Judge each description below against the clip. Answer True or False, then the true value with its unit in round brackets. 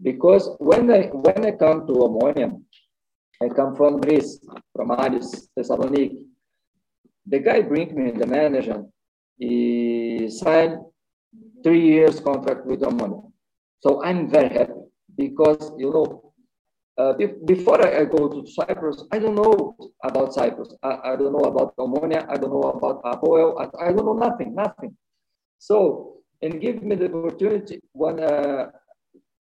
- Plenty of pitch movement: True (6.7 semitones)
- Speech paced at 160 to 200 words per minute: False (145 wpm)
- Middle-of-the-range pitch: True (155 Hz)